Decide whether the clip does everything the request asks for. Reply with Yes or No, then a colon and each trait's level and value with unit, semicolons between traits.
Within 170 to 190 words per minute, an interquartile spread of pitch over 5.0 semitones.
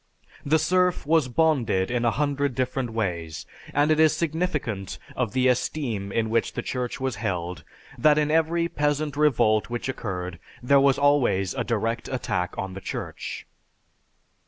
No: average, 155 wpm; wide, 5.4 semitones